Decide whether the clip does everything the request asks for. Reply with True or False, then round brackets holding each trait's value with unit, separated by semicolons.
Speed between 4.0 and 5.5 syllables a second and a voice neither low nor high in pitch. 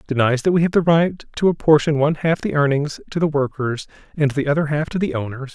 False (6.2 syllables/s; 145 Hz)